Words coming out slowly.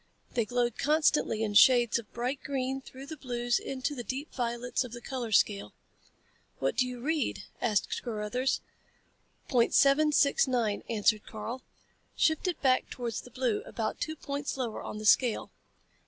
No: average, 165 wpm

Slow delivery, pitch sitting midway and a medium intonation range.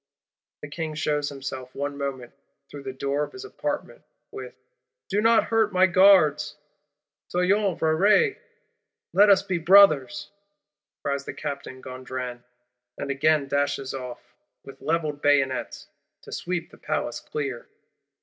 Yes: slow, 125 wpm; medium, 150 Hz; average, 5.0 semitones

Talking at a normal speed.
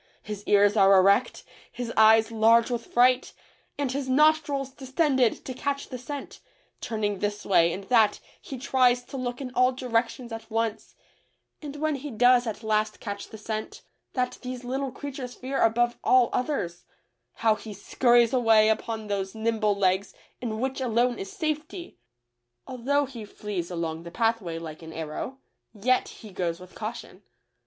Yes: average, 165 wpm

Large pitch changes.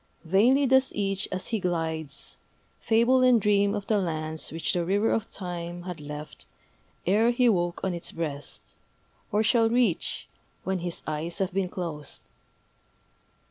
No: average, 4.6 semitones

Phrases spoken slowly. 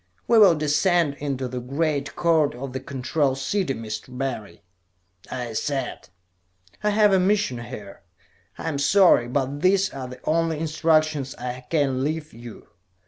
No: average, 150 wpm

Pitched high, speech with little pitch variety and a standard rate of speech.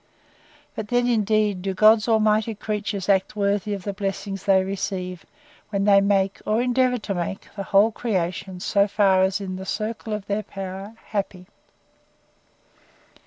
Yes: high, 200 Hz; narrow, 1.9 semitones; average, 160 wpm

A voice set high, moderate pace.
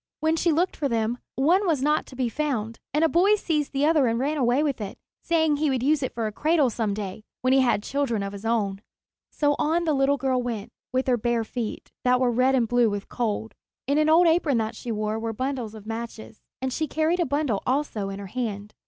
No: very high, 255 Hz; fast, 240 wpm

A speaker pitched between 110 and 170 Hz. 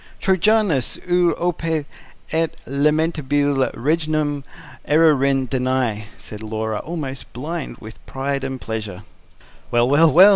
Yes: medium, 140 Hz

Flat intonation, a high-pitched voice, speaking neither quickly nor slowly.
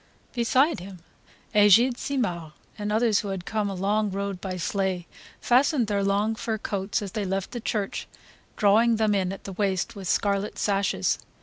Yes: narrow, 2.2 semitones; high, 200 Hz; average, 175 wpm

